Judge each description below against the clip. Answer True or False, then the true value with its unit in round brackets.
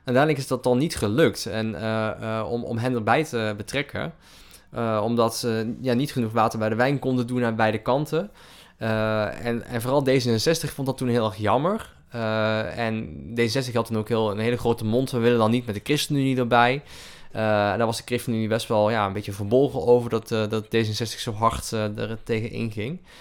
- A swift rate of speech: True (215 wpm)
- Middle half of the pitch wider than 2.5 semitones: False (2.1 semitones)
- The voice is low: True (115 Hz)